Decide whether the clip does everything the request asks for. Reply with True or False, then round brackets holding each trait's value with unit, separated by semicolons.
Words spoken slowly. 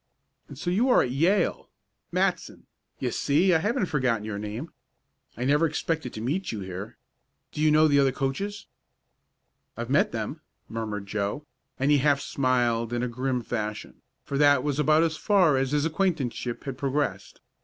False (175 wpm)